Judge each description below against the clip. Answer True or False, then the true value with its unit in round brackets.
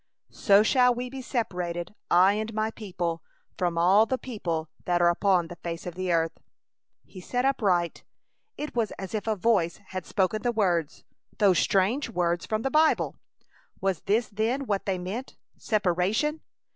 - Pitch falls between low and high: False (200 Hz)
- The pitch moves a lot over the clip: False (4.4 semitones)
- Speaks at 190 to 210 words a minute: False (170 wpm)